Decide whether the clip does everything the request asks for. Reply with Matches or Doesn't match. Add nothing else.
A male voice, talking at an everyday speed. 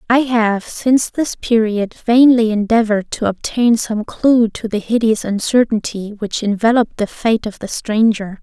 Doesn't match